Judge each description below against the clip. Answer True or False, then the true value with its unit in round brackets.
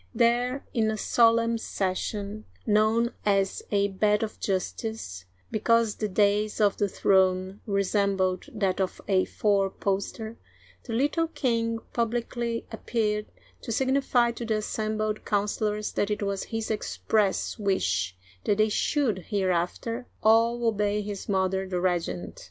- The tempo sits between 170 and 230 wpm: False (140 wpm)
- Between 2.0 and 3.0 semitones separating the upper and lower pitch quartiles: True (2.6 semitones)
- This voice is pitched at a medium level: False (210 Hz)